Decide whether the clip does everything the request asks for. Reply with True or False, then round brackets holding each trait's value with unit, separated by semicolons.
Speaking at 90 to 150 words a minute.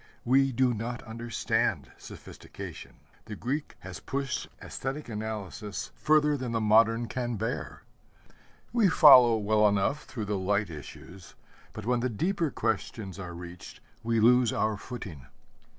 True (135 wpm)